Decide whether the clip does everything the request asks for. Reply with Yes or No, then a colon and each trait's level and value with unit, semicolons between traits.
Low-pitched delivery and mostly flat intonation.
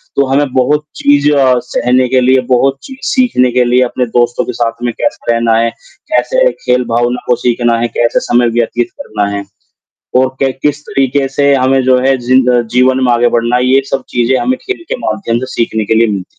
Yes: low, 125 Hz; narrow, 2.2 semitones